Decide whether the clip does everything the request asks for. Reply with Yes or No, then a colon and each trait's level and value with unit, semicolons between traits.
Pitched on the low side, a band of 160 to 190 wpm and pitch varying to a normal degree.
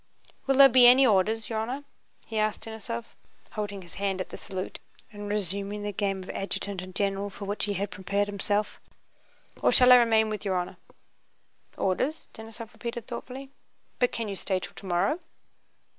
No: high, 205 Hz; average, 175 wpm; average, 3.0 semitones